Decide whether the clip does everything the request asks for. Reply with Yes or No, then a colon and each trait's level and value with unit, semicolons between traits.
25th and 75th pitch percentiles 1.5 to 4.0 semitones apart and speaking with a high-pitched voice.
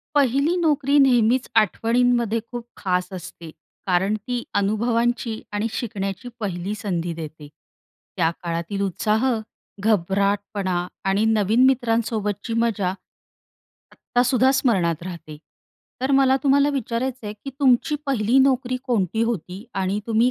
No: average, 4.4 semitones; high, 220 Hz